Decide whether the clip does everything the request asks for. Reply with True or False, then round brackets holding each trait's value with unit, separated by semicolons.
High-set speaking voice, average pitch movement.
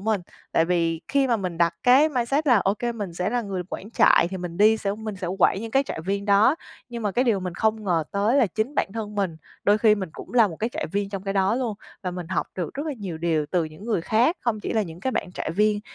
True (205 Hz; 4.0 semitones)